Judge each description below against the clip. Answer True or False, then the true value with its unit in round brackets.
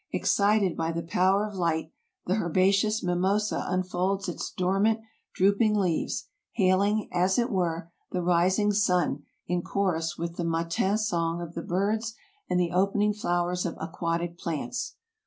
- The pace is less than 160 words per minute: True (145 wpm)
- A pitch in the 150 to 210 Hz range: True (185 Hz)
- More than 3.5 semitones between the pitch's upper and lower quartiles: False (3.0 semitones)